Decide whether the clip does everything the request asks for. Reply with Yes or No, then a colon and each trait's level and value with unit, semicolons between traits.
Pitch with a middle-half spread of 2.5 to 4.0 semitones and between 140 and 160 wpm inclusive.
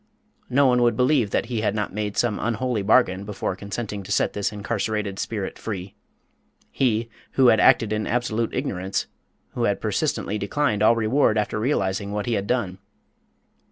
No: average, 3.0 semitones; average, 170 wpm